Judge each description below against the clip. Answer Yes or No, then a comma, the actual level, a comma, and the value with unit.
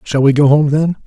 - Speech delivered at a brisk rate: Yes, fast, 280 wpm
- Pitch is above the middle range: No, medium, 145 Hz